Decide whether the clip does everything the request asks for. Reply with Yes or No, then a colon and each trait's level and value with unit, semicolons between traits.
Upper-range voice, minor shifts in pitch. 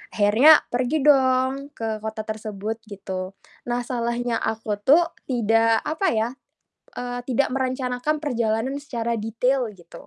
No: high, 240 Hz; average, 3.2 semitones